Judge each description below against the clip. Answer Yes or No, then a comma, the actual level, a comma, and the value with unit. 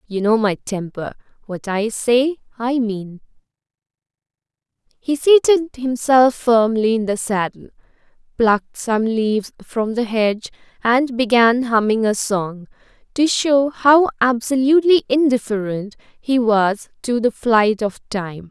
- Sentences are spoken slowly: Yes, slow, 125 wpm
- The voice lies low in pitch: No, high, 235 Hz